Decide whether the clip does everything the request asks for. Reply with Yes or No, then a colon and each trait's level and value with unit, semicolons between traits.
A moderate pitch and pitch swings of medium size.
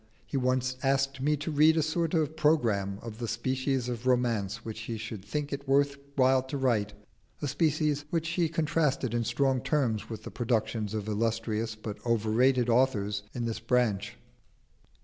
No: low, 125 Hz; average, 4.2 semitones